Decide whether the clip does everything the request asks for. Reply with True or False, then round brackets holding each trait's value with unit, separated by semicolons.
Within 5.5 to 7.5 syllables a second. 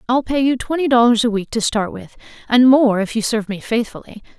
True (5.9 syllables/s)